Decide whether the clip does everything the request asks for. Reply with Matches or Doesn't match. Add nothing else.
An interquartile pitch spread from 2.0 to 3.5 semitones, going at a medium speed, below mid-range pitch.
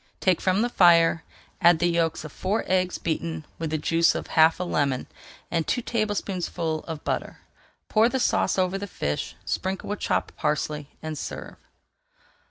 Doesn't match